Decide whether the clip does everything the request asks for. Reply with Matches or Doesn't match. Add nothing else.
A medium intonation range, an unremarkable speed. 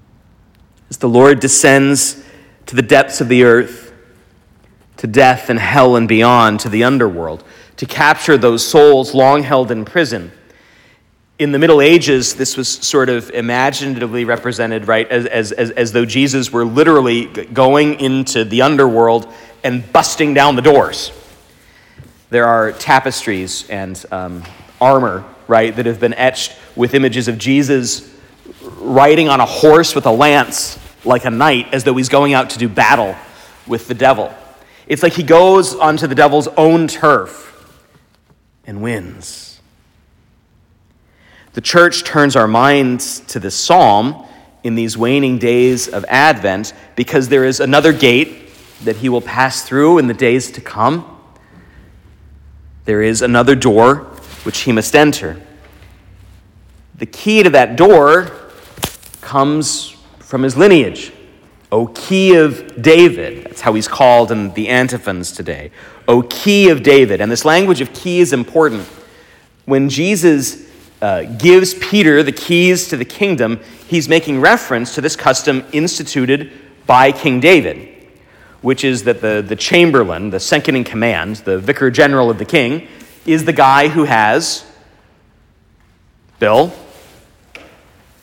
Matches